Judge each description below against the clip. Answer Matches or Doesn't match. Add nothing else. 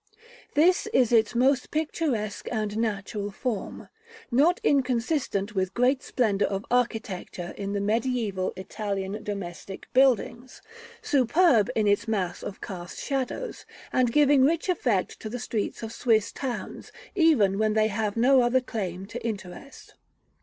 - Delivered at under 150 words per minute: Matches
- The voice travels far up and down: Doesn't match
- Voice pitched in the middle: Doesn't match